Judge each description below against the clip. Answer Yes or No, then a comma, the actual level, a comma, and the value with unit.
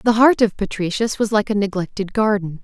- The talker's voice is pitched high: Yes, high, 205 Hz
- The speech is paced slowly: No, fast, 205 wpm